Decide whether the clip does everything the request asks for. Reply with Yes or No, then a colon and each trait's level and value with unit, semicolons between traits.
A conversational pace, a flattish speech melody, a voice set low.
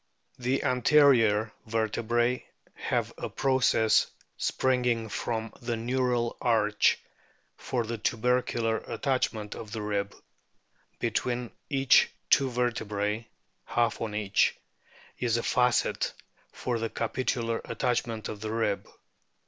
No: slow, 110 wpm; narrow, 2.1 semitones; low, 115 Hz